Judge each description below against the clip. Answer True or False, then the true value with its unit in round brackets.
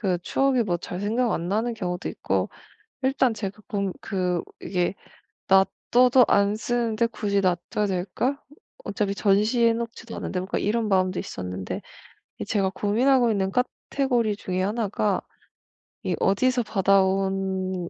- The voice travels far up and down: False (3.7 semitones)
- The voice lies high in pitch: True (205 Hz)